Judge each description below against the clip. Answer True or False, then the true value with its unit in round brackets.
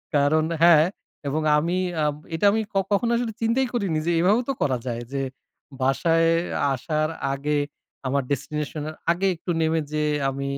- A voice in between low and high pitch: True (155 Hz)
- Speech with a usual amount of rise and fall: True (4.1 semitones)